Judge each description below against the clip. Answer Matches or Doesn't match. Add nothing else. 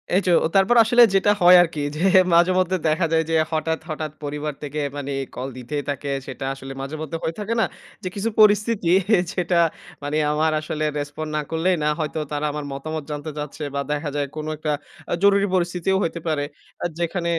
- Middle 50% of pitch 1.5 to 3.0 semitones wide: Doesn't match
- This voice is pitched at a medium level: Matches